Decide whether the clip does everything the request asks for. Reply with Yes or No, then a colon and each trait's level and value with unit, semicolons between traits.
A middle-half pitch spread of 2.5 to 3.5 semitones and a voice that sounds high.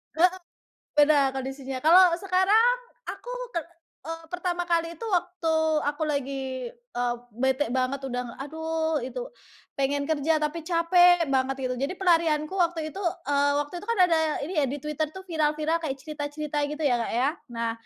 No: average, 4.0 semitones; very high, 305 Hz